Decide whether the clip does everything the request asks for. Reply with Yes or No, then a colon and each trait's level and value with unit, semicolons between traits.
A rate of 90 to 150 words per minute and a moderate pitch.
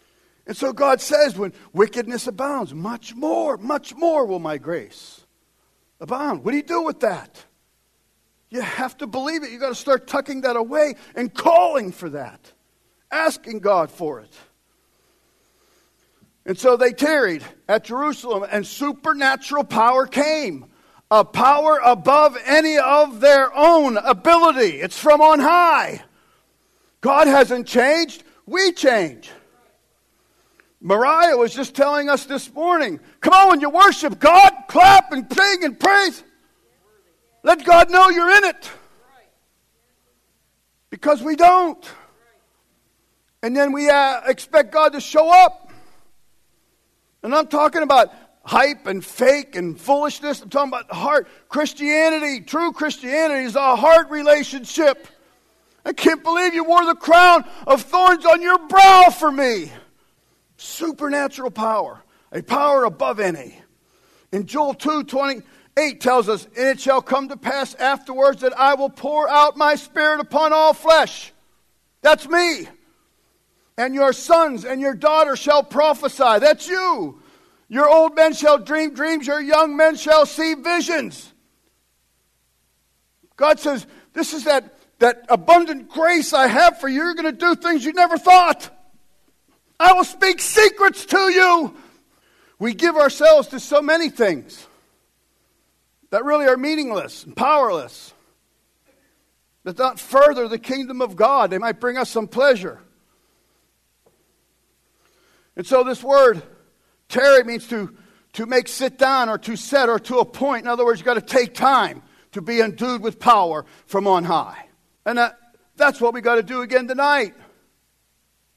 No: average, 145 wpm; very high, 285 Hz